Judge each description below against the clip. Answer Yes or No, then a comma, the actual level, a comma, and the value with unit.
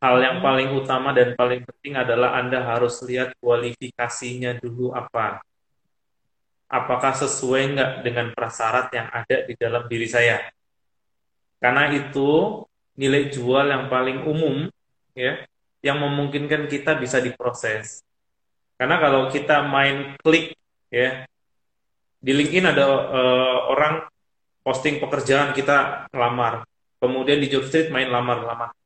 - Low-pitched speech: Yes, low, 130 Hz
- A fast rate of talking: No, average, 120 wpm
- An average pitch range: No, narrow, 2.3 semitones